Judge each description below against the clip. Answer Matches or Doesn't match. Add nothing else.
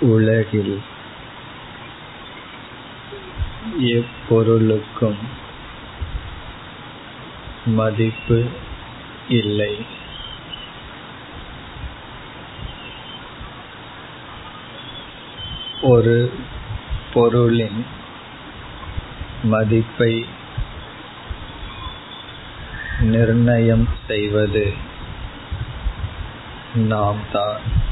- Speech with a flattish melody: Matches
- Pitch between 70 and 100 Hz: Doesn't match